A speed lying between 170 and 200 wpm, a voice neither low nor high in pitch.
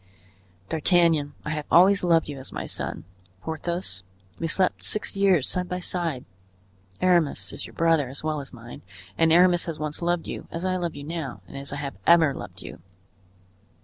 Yes: average, 185 wpm; medium, 165 Hz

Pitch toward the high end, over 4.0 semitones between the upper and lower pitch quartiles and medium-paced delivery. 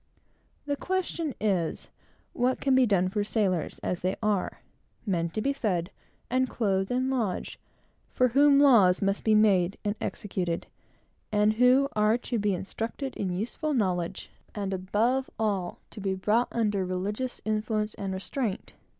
Yes: high, 210 Hz; average, 4.6 semitones; average, 150 wpm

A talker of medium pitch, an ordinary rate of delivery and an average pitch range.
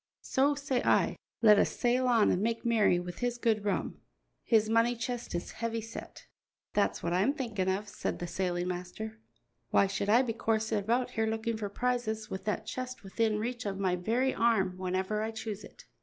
No: high, 220 Hz; average, 195 wpm; average, 3.1 semitones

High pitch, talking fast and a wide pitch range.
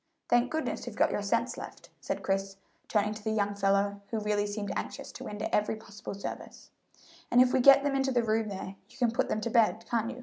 No: high, 215 Hz; fast, 235 wpm; average, 3.0 semitones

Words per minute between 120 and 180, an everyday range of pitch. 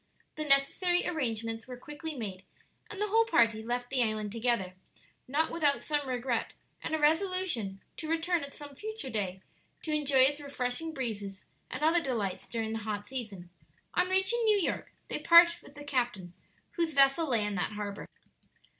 No: average, 170 wpm; wide, 6.5 semitones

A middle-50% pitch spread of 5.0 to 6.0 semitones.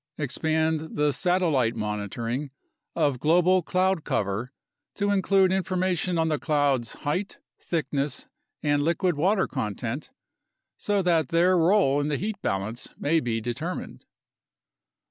Yes: wide, 5.6 semitones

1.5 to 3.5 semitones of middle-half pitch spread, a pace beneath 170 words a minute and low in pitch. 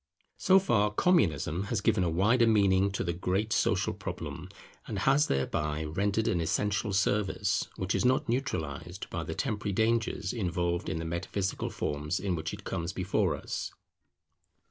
No: average, 4.1 semitones; average, 160 wpm; very low, 95 Hz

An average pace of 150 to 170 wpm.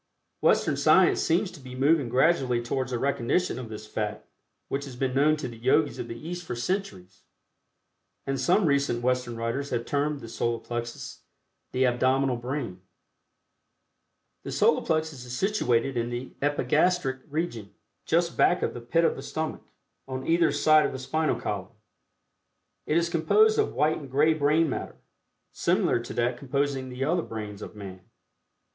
Yes: average, 165 wpm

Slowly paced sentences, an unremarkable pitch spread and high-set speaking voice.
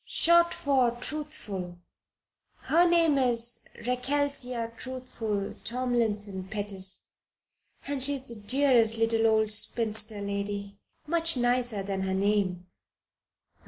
Yes: slow, 105 wpm; average, 4.3 semitones; high, 230 Hz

